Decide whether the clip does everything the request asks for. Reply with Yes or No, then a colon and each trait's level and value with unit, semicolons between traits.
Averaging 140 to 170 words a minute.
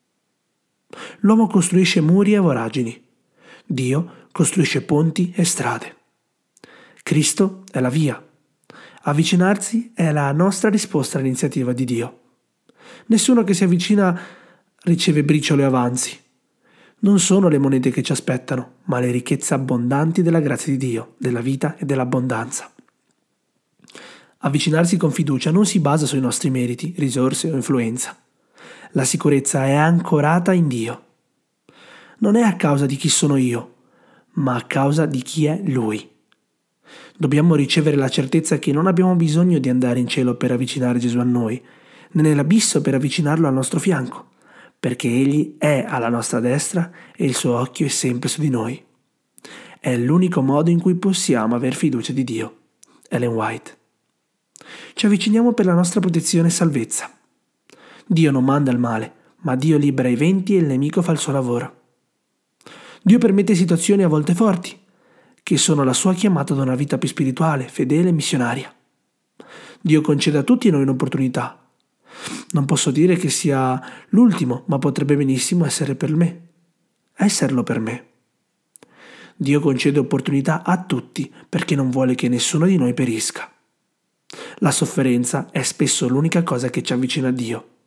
Yes: average, 150 wpm